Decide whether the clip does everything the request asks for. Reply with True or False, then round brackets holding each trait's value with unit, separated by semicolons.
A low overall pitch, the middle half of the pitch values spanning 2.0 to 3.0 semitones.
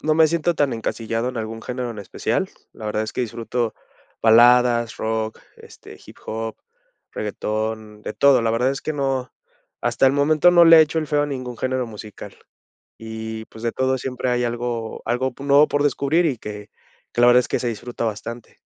False (120 Hz; 3.4 semitones)